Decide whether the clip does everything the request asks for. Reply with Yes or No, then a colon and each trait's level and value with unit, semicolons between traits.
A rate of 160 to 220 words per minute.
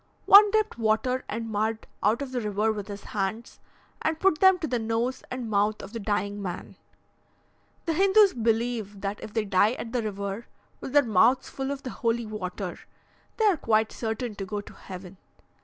Yes: average, 190 wpm